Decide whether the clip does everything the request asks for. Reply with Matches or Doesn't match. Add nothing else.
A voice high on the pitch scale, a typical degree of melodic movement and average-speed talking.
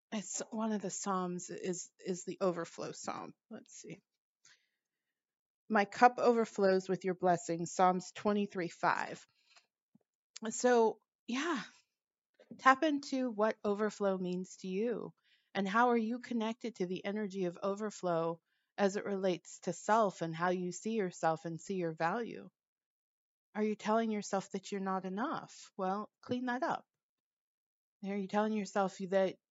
Matches